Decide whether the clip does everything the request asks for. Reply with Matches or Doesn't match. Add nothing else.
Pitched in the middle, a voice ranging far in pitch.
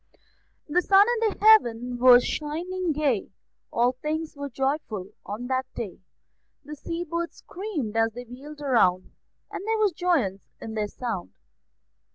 Doesn't match